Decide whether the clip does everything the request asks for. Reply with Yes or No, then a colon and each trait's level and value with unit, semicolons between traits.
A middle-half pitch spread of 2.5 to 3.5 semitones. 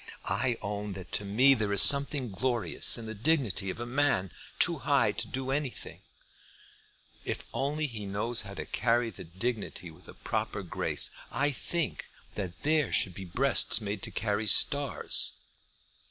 No: average, 5.3 semitones